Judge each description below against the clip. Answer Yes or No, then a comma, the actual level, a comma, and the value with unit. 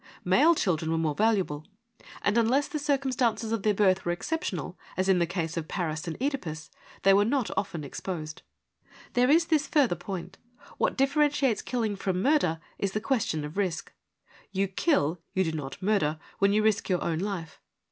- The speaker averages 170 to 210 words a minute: Yes, average, 180 wpm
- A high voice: Yes, high, 195 Hz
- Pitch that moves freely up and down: Yes, wide, 6.7 semitones